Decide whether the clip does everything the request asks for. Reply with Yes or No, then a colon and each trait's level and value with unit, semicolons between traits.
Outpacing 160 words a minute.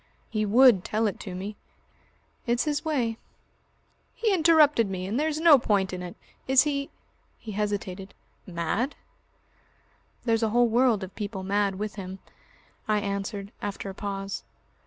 No: average, 155 wpm